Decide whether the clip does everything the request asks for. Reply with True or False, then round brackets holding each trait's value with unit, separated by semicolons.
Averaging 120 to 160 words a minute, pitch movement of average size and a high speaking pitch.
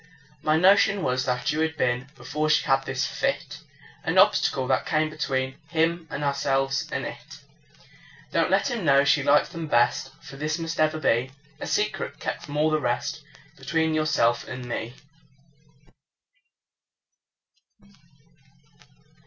False (145 wpm; 3.2 semitones; 150 Hz)